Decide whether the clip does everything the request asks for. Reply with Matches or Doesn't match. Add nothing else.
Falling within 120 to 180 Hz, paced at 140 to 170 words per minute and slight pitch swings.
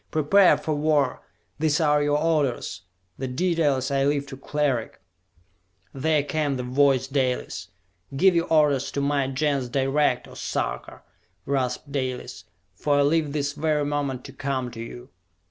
Matches